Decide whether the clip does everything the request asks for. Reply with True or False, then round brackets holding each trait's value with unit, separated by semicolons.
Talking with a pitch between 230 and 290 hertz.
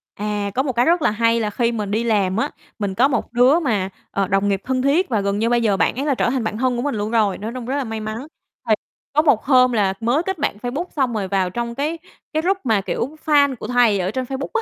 True (235 Hz)